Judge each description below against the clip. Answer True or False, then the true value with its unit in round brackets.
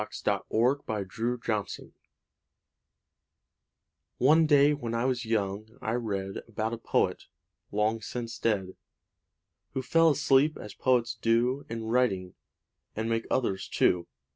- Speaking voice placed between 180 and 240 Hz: False (115 Hz)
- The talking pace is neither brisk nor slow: False (130 wpm)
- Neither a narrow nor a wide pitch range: True (3.2 semitones)